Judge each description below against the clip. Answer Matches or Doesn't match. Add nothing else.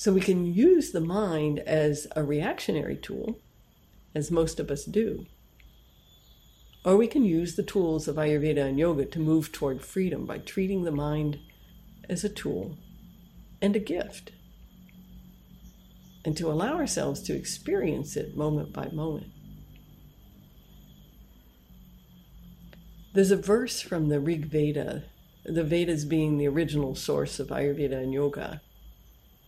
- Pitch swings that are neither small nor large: Matches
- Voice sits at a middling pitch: Matches